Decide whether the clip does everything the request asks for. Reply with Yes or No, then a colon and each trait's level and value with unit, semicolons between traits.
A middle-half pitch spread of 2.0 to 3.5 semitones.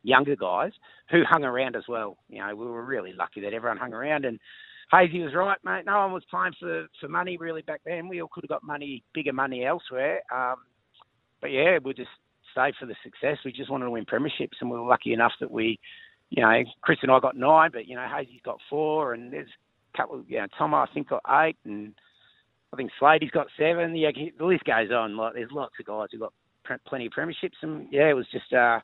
No: average, 5.0 semitones